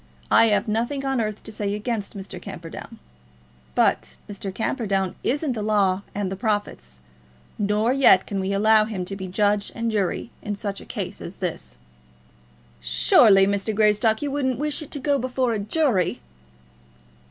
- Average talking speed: Yes, average, 165 wpm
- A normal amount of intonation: Yes, average, 3.0 semitones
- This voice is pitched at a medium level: No, high, 210 Hz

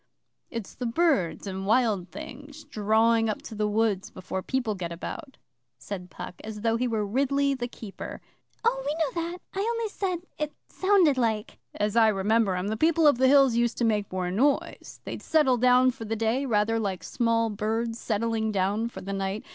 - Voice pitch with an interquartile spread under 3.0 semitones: No, average, 4.5 semitones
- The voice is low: No, high, 230 Hz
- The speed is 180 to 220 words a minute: Yes, average, 195 wpm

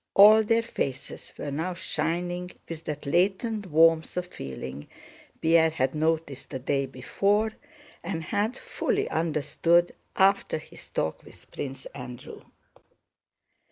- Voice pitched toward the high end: No, medium, 165 Hz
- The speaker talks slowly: Yes, slow, 125 wpm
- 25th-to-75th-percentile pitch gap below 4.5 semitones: No, average, 5.1 semitones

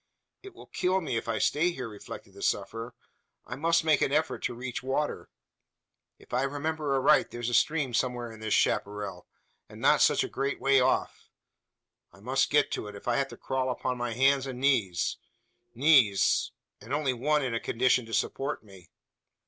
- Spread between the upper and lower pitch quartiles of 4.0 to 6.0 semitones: No, average, 3.6 semitones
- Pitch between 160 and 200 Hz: No, low, 130 Hz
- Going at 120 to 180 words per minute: No, average, 190 wpm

